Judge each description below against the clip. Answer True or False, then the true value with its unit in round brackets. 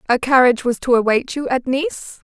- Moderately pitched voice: False (245 Hz)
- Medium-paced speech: False (210 wpm)